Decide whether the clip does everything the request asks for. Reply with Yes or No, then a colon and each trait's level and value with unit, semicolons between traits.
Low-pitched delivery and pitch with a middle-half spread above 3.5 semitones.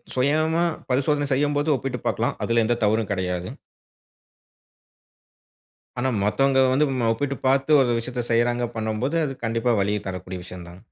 Yes: low, 120 Hz; average, 4.2 semitones